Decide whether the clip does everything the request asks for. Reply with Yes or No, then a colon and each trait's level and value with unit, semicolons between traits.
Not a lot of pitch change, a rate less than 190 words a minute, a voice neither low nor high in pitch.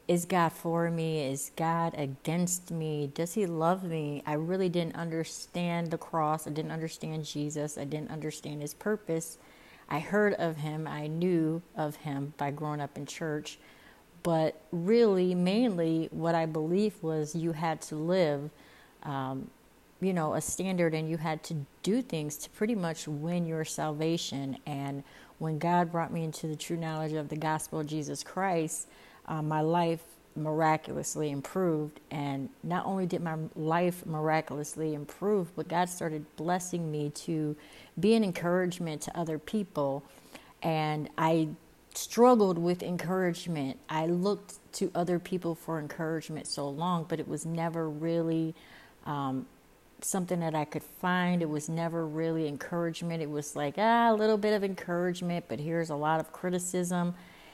Yes: narrow, 2.3 semitones; average, 160 wpm; medium, 160 Hz